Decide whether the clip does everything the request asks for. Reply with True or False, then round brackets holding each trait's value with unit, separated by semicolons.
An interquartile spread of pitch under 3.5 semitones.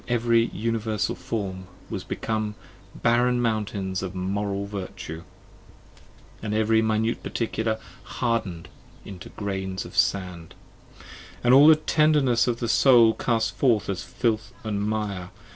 True (2.9 semitones)